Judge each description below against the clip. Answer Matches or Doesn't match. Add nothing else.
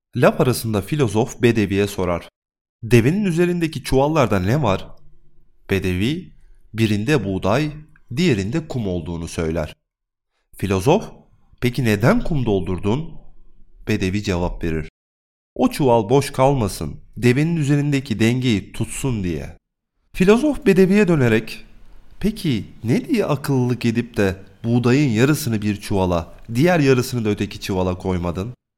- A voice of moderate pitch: Doesn't match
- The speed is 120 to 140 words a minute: Doesn't match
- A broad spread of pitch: Matches